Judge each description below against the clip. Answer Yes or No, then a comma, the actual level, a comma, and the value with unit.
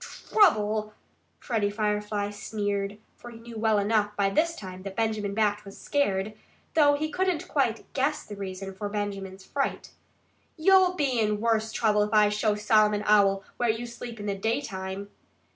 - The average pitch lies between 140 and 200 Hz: No, high, 210 Hz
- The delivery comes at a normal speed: Yes, average, 165 wpm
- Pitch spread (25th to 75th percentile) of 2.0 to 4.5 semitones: Yes, narrow, 2.4 semitones